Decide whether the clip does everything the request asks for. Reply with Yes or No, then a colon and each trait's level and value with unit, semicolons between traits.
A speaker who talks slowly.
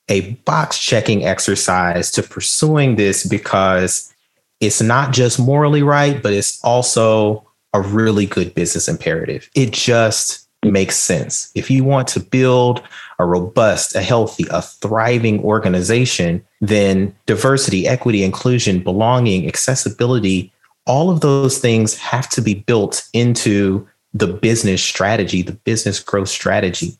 Yes: slow, 130 wpm